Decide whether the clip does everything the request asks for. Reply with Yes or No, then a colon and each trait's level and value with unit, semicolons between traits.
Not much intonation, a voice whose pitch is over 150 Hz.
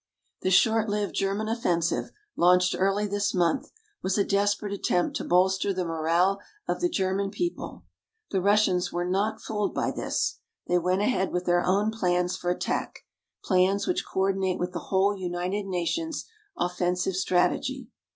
Yes: narrow, 2.2 semitones; high, 190 Hz